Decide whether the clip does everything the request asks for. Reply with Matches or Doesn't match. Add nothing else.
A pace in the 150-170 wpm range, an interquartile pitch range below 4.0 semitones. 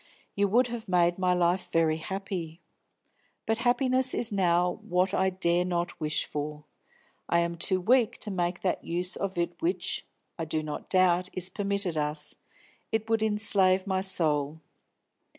Matches